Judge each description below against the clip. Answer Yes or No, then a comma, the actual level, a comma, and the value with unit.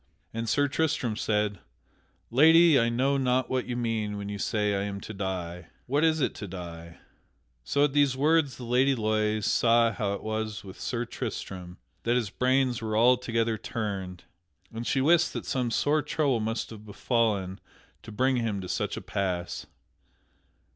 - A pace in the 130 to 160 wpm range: No, average, 175 wpm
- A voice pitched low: Yes, low, 115 Hz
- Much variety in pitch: No, average, 4.1 semitones